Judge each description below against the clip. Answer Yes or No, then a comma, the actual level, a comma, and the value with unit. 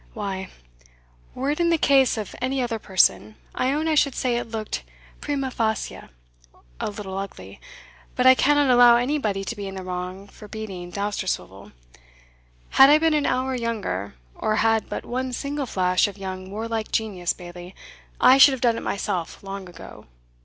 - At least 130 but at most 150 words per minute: No, average, 175 wpm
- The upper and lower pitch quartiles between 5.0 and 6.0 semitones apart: Yes, average, 5.3 semitones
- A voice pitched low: No, high, 220 Hz